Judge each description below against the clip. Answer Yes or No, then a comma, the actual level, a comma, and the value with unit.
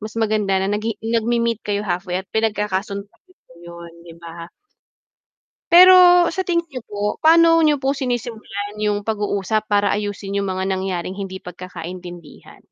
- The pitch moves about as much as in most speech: Yes, average, 3.5 semitones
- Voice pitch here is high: Yes, high, 205 Hz